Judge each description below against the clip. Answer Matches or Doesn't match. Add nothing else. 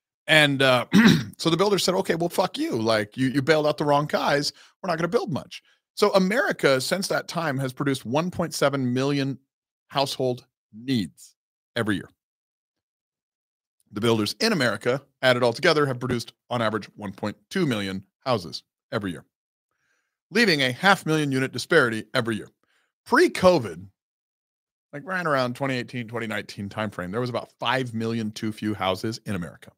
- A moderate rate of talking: Matches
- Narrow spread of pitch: Doesn't match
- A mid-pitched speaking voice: Doesn't match